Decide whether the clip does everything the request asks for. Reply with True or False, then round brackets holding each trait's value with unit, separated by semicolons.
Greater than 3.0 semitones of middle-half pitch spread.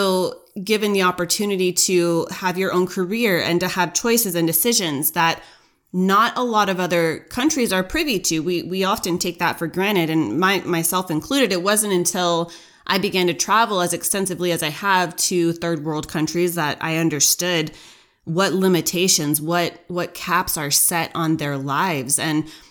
False (2.5 semitones)